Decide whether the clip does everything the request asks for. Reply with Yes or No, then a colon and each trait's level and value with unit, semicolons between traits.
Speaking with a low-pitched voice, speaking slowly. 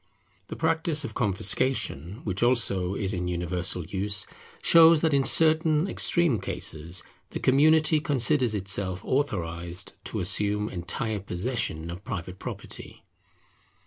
Yes: low, 105 Hz; slow, 120 wpm